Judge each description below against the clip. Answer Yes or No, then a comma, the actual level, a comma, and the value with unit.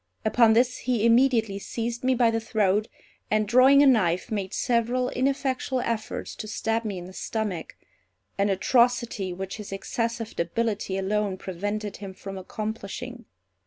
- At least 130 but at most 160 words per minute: Yes, average, 150 wpm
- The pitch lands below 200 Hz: No, high, 220 Hz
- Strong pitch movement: No, average, 3.4 semitones